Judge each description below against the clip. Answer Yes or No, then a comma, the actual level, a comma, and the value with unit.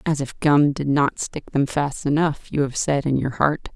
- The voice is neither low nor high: Yes, medium, 145 Hz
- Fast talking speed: Yes, fast, 240 wpm